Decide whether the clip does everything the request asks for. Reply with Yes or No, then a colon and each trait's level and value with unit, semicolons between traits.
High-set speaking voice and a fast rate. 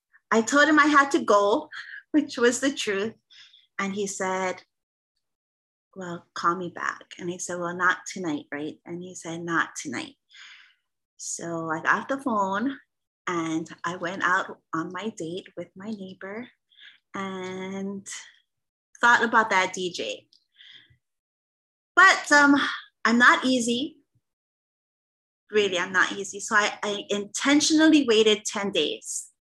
No: high, 205 Hz; slow, 135 wpm